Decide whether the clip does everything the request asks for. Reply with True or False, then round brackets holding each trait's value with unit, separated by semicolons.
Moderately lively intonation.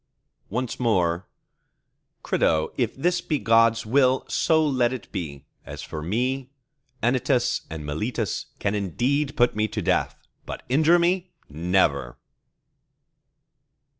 False (6.6 semitones)